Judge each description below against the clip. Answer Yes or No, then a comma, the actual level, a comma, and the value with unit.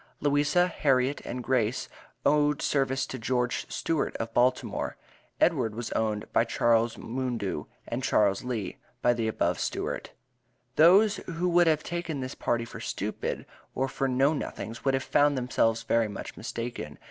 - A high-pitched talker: No, low, 125 Hz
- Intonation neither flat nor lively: Yes, average, 4.0 semitones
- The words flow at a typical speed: Yes, average, 155 wpm